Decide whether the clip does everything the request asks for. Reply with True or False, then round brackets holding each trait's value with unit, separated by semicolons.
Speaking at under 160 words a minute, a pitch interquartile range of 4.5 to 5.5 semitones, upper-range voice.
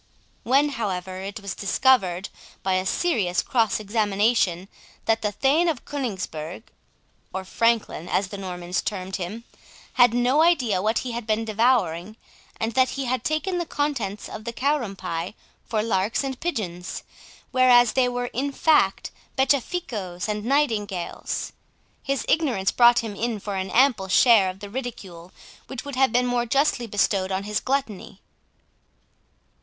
True (150 wpm; 5.0 semitones; 225 Hz)